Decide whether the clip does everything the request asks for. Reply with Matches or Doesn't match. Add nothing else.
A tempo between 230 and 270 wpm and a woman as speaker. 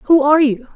Matches